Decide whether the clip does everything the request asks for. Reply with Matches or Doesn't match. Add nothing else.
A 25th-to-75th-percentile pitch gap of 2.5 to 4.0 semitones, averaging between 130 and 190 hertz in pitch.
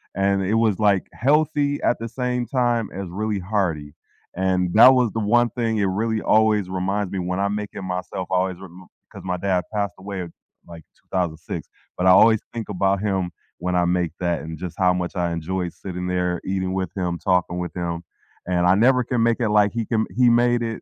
Doesn't match